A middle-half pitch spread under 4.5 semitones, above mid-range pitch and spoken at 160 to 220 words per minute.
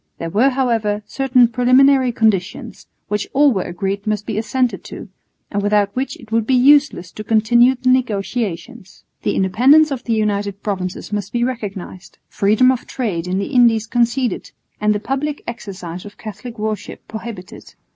Yes: average, 3.8 semitones; high, 220 Hz; average, 165 wpm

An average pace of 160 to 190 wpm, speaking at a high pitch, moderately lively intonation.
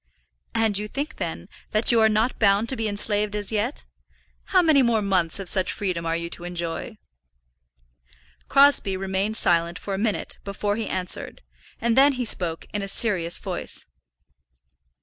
Yes: average, 170 wpm; high, 205 Hz; average, 3.3 semitones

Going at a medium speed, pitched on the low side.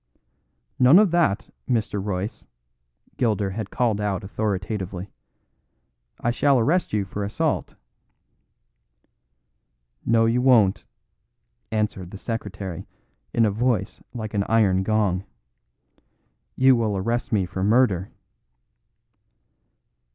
No: slow, 105 wpm; low, 105 Hz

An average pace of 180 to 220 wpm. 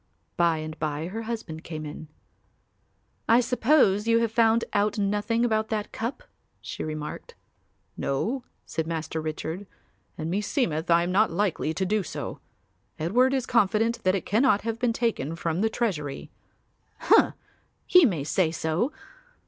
No: average, 150 wpm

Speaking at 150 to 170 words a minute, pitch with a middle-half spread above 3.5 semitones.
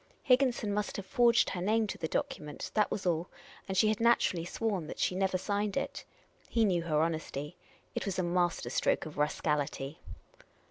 No: average, 185 wpm; average, 4.5 semitones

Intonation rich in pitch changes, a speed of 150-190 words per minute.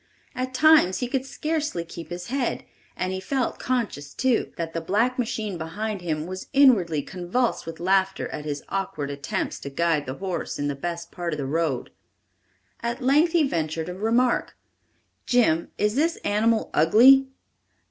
Yes: wide, 7.3 semitones; average, 170 wpm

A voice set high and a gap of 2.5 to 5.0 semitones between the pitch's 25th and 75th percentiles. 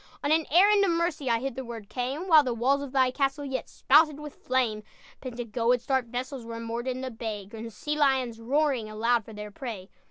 Yes: very high, 255 Hz; average, 3.6 semitones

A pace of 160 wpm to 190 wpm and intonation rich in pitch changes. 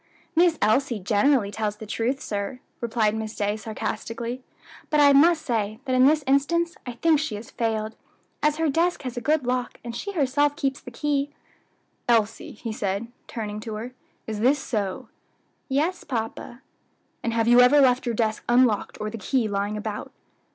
No: average, 180 wpm; average, 4.5 semitones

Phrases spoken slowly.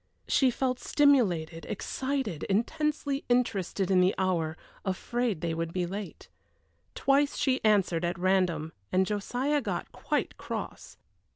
Yes: slow, 125 wpm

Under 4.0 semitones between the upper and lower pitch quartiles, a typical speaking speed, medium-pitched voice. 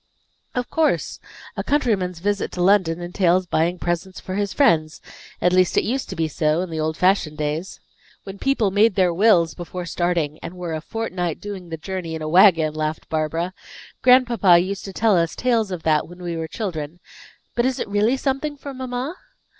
No: average, 4.3 semitones; average, 195 wpm; medium, 180 Hz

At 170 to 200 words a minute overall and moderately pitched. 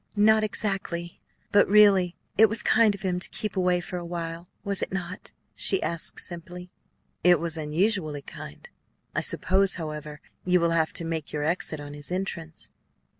Yes: average, 175 wpm; medium, 175 Hz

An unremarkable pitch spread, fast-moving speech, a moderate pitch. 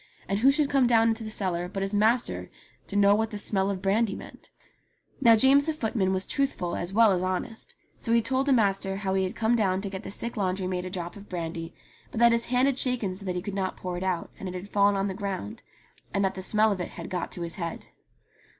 No: average, 3.5 semitones; fast, 260 wpm; high, 200 Hz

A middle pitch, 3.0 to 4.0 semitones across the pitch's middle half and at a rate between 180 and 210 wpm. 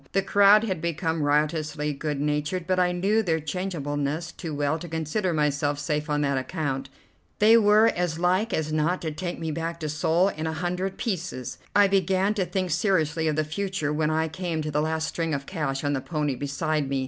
Yes: medium, 160 Hz; average, 3.6 semitones; fast, 205 wpm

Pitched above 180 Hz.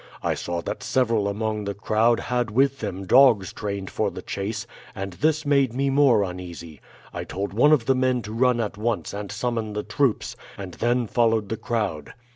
No: low, 110 Hz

